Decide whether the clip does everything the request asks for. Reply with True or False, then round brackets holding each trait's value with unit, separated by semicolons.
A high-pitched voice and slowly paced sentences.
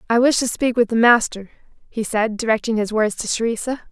False (230 Hz; 200 wpm)